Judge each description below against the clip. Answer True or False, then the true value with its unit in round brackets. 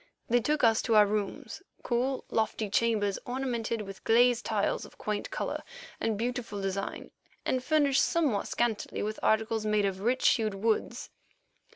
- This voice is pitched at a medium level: False (225 Hz)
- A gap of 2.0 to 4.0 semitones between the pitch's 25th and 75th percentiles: True (2.7 semitones)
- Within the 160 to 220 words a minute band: False (150 wpm)